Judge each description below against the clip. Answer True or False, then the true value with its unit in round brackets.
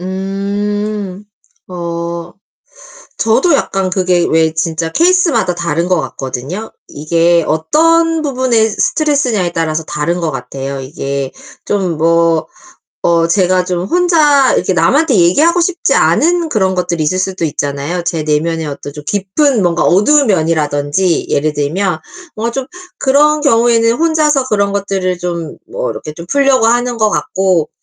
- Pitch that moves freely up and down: True (6.7 semitones)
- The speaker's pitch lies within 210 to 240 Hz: False (185 Hz)